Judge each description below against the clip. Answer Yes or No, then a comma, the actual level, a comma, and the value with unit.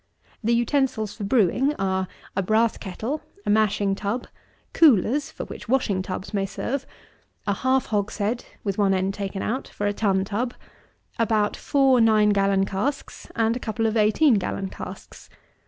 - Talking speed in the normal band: Yes, average, 160 wpm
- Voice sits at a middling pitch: No, high, 215 Hz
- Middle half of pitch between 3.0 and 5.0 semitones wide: Yes, average, 3.6 semitones